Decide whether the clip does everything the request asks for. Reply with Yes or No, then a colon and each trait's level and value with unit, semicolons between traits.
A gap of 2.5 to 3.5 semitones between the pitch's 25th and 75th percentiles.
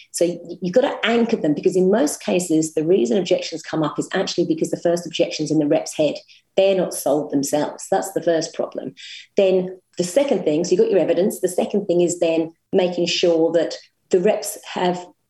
Yes: average, 2.9 semitones